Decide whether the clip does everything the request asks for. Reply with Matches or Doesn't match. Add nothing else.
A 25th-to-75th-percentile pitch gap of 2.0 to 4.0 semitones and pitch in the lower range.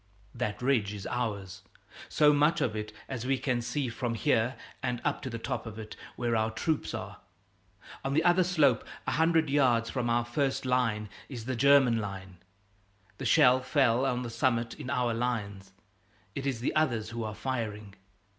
Matches